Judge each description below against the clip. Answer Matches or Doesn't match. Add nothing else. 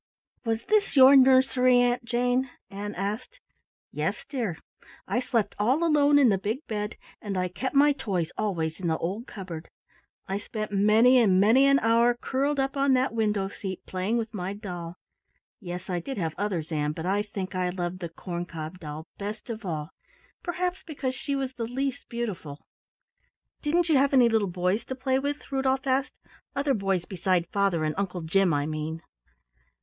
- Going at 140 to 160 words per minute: Doesn't match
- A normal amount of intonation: Doesn't match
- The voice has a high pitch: Matches